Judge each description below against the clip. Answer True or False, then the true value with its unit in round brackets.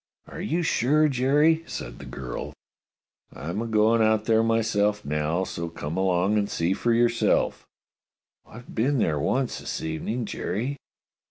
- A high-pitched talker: False (110 Hz)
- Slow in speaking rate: False (160 wpm)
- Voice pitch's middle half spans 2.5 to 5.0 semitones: False (5.5 semitones)